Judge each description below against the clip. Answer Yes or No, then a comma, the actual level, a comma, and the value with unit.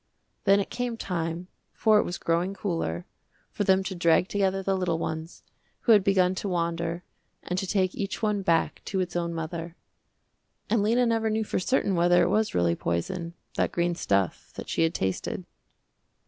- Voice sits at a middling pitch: Yes, medium, 180 Hz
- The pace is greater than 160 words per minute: Yes, average, 185 wpm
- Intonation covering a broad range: No, average, 3.0 semitones